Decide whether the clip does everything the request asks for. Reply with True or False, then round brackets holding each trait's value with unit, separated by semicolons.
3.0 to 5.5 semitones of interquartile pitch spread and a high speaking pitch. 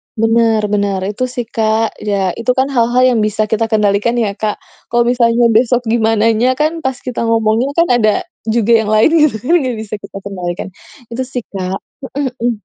False (2.5 semitones; 230 Hz)